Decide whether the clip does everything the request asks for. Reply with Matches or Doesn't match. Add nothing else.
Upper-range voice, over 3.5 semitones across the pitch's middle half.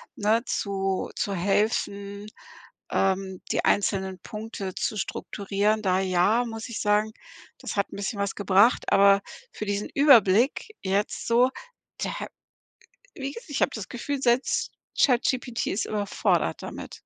Doesn't match